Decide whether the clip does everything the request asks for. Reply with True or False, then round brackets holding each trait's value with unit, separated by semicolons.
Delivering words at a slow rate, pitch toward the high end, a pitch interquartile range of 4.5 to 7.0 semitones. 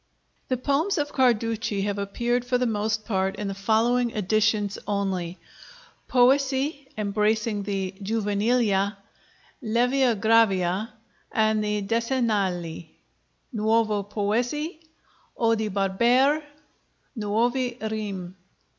False (95 wpm; 220 Hz; 3.3 semitones)